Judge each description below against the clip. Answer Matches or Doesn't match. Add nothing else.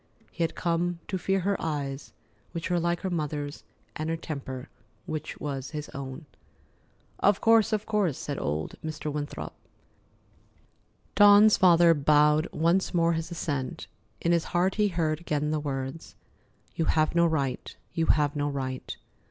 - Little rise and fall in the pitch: Doesn't match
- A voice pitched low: Doesn't match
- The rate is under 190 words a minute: Matches